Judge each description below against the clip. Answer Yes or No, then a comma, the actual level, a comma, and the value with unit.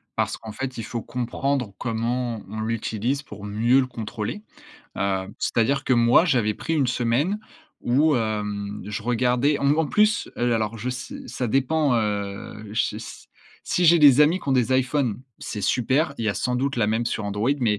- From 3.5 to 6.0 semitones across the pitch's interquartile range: Yes, average, 4.0 semitones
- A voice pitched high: No, low, 120 Hz